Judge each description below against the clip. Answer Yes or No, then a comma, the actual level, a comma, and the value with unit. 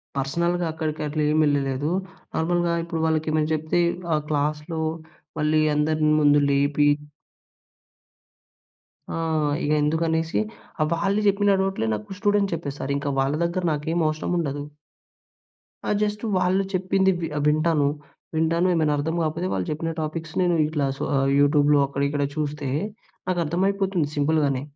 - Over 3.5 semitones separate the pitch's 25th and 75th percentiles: No, average, 2.8 semitones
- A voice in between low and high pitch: Yes, medium, 155 Hz